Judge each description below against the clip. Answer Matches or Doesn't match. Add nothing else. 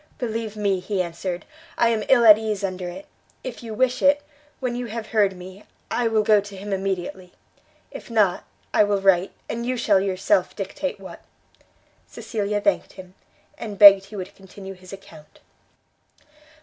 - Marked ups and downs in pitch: Doesn't match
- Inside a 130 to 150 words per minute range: Doesn't match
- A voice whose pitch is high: Matches